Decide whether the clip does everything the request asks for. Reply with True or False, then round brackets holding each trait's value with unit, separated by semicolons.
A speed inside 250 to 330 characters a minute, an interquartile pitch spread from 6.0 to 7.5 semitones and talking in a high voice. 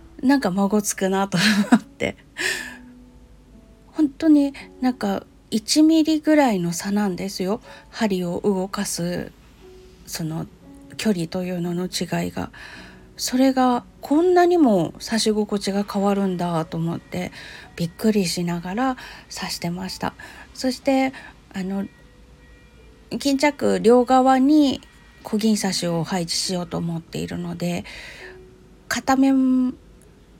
False (225 characters per minute; 6.7 semitones; 205 Hz)